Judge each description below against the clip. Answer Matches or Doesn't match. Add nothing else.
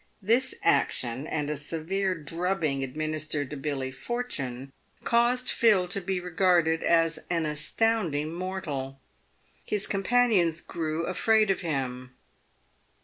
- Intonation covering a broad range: Doesn't match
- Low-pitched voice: Doesn't match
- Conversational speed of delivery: Doesn't match